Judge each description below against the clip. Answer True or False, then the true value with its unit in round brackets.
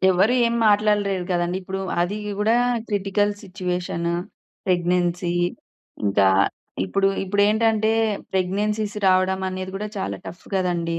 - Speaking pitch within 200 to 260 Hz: False (190 Hz)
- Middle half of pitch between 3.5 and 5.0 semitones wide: False (2.6 semitones)